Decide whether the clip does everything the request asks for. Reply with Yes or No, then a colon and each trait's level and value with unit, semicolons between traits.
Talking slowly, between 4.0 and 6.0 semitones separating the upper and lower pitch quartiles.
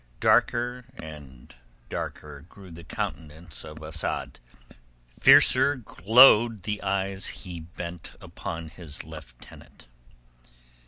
Yes: slow, 95 wpm; average, 4.7 semitones